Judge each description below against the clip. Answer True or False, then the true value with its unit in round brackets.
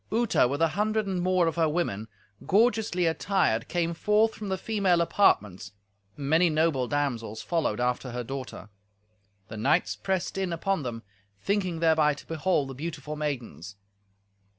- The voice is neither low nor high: True (160 Hz)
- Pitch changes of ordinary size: False (6.8 semitones)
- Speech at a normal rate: True (155 wpm)